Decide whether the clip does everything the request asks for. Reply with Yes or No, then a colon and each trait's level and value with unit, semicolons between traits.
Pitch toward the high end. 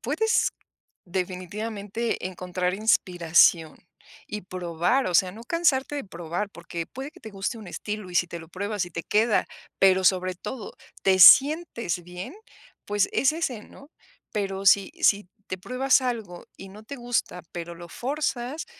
Yes: high, 200 Hz